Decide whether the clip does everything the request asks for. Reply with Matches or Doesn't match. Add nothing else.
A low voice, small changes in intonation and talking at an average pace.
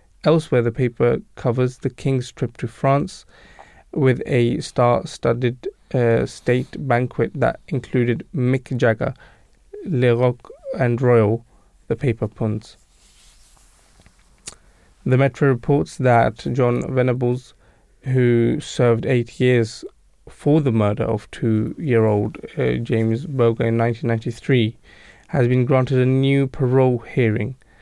Doesn't match